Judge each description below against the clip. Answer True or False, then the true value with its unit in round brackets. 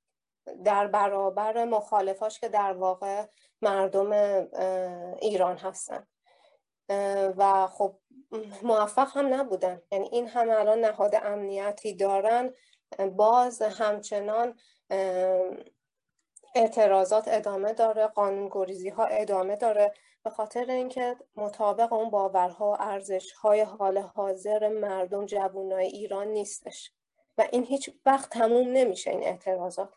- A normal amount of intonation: False (2.3 semitones)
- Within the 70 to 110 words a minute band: True (105 wpm)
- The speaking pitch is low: False (205 Hz)